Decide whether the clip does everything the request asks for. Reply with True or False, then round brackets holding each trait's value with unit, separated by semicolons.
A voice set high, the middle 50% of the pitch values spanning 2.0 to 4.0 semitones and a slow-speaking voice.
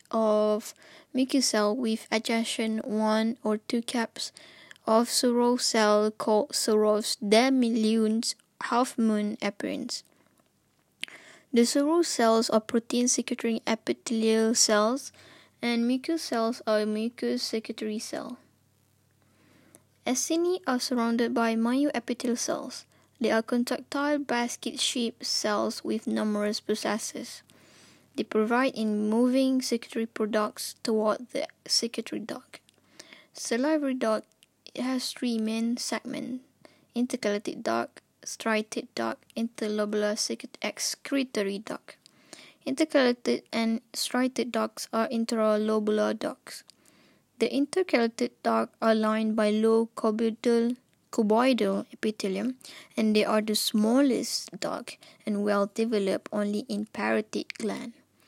True (230 Hz; 2.8 semitones; 105 wpm)